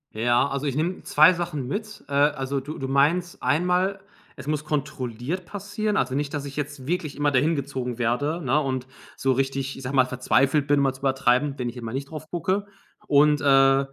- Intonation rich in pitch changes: No, average, 2.7 semitones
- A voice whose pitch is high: No, medium, 140 Hz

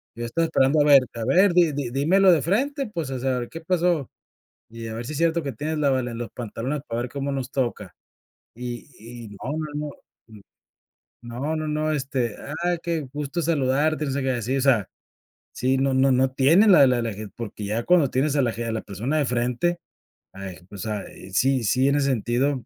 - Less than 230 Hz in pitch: Yes, low, 135 Hz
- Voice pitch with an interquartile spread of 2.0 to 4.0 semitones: No, average, 4.4 semitones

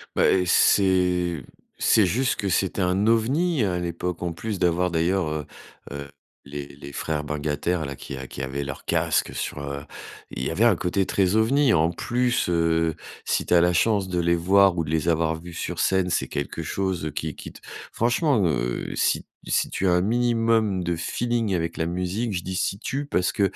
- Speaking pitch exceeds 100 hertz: No, very low, 90 Hz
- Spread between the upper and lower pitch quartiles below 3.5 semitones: No, average, 3.8 semitones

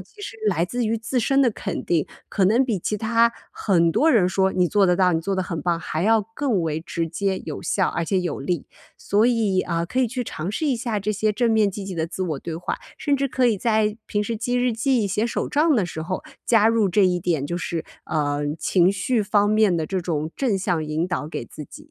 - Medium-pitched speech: No, high, 200 Hz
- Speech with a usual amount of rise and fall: Yes, average, 4.8 semitones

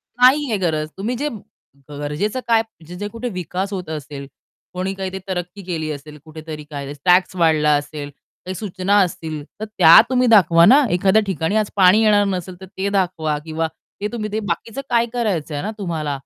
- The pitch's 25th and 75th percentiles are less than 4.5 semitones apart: No, average, 5.0 semitones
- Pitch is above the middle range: No, medium, 180 Hz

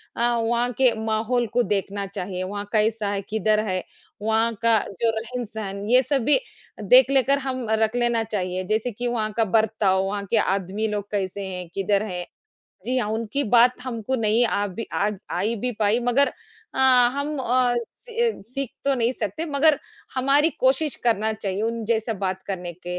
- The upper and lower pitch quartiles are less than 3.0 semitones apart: No, average, 3.4 semitones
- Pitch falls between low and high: No, high, 225 Hz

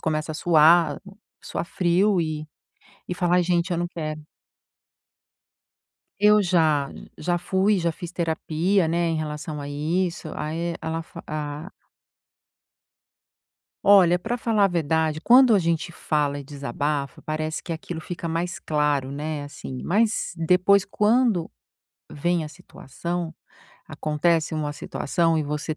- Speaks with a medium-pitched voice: Yes, medium, 165 Hz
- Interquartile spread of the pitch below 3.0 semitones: Yes, narrow, 2.6 semitones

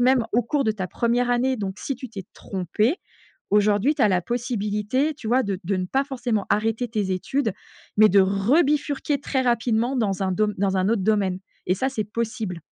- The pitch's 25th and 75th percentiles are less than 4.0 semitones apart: No, average, 4.3 semitones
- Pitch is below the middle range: No, high, 220 Hz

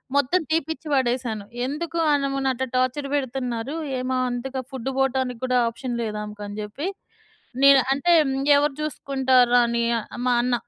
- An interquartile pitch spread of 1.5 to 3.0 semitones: Yes, narrow, 2.4 semitones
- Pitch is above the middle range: Yes, very high, 260 Hz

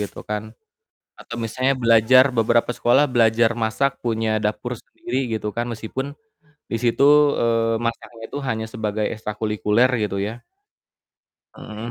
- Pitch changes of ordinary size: No, narrow, 1.6 semitones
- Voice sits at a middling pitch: No, low, 115 Hz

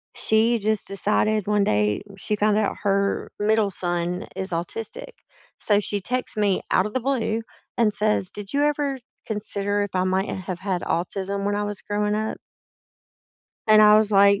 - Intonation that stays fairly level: Yes, narrow, 1.8 semitones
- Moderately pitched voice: No, high, 205 Hz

